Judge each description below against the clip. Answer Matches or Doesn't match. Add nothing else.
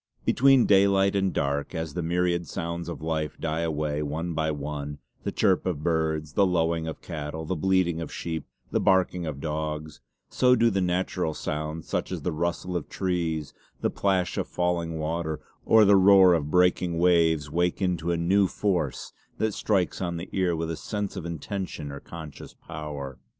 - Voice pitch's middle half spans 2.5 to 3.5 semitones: Matches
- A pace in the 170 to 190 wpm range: Matches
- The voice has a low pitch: Matches